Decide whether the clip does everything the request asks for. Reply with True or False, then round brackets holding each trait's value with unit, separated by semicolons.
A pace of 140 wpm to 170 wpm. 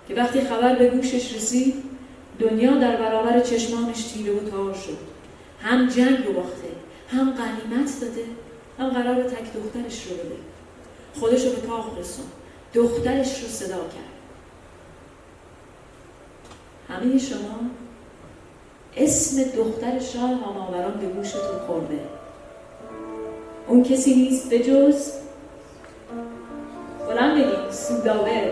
False (110 wpm)